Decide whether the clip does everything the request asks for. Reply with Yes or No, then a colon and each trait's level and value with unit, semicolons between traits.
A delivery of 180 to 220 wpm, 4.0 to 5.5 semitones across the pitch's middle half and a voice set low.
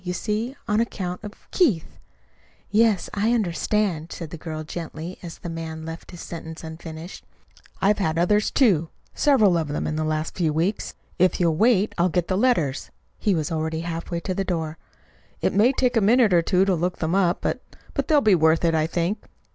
No: average, 200 wpm; average, 4.4 semitones; medium, 175 Hz